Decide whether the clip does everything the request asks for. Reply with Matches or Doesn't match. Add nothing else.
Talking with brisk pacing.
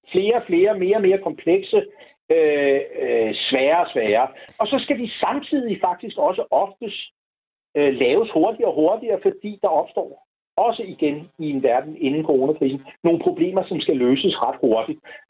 Doesn't match